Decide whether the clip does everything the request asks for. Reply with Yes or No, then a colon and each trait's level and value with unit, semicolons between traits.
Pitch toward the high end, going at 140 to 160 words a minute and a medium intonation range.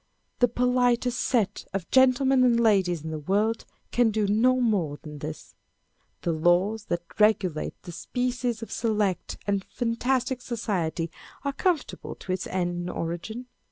No: high, 215 Hz; average, 150 wpm; wide, 5.8 semitones